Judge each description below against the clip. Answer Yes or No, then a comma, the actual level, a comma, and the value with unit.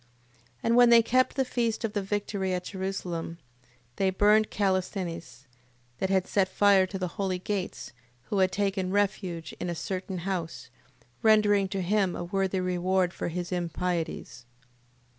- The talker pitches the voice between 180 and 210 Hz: Yes, high, 190 Hz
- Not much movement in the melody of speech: Yes, narrow, 2.3 semitones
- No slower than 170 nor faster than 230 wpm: No, average, 160 wpm